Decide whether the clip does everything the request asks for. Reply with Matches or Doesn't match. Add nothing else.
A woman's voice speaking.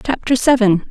Matches